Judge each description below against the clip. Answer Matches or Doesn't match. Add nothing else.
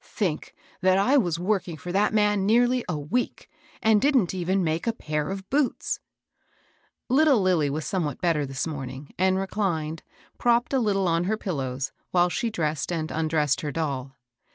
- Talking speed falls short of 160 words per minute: Doesn't match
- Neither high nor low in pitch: Matches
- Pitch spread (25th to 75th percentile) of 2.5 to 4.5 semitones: Doesn't match